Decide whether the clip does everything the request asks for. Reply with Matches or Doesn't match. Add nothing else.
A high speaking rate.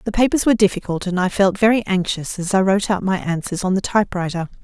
Matches